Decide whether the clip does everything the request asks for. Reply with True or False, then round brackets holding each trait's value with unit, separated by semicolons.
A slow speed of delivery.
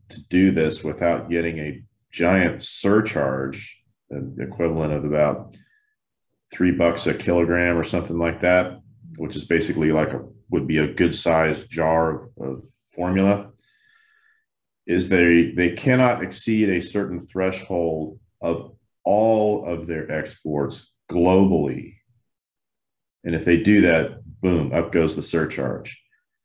True (130 wpm)